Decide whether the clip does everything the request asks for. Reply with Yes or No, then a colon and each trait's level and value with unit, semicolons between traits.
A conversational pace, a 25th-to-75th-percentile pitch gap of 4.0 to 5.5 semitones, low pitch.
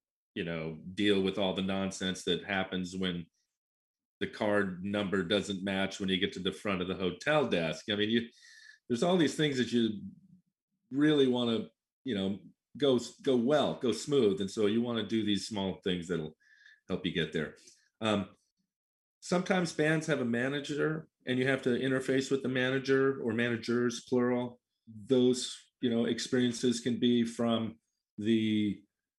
Yes: average, 170 wpm; average, 5.1 semitones; low, 115 Hz